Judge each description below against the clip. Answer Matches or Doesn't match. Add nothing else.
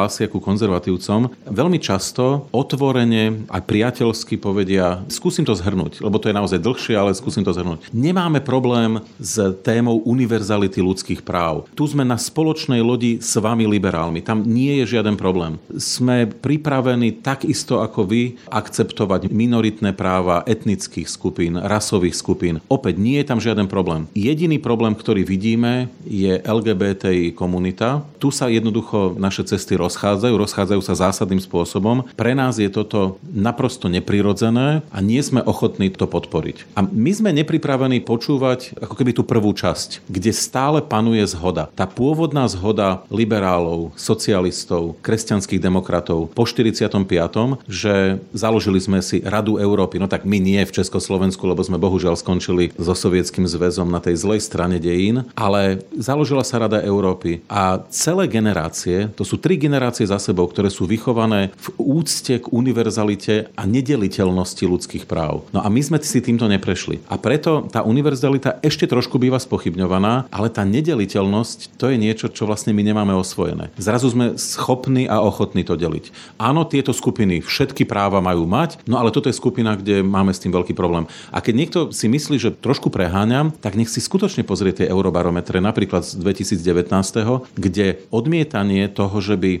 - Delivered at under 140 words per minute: Doesn't match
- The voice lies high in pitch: Doesn't match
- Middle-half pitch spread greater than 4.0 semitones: Matches